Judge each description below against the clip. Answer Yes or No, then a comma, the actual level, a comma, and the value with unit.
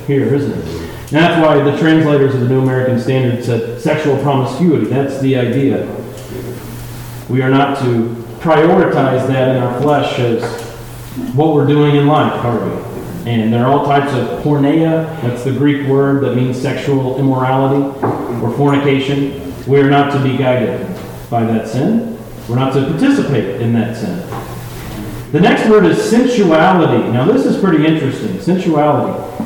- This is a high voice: No, low, 135 Hz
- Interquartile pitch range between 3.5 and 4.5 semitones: No, average, 3.1 semitones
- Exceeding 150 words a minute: Yes, average, 165 wpm